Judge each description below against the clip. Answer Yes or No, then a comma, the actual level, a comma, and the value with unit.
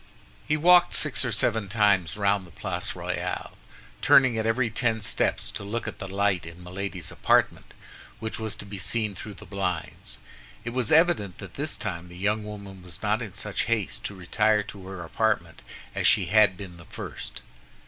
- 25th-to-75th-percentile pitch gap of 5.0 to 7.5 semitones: No, average, 3.1 semitones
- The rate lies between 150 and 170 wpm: No, average, 190 wpm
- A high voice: No, low, 105 Hz